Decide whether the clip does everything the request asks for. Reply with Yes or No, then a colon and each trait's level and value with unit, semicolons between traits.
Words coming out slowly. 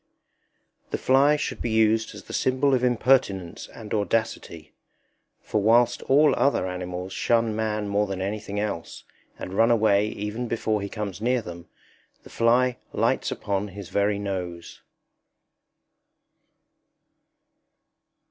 Yes: slow, 130 wpm